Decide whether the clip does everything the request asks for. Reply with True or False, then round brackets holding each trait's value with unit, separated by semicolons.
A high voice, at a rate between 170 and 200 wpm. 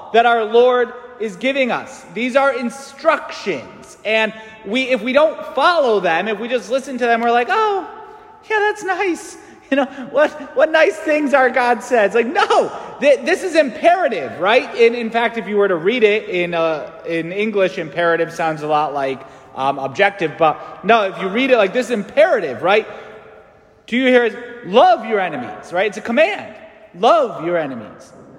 True (240 Hz; 180 wpm)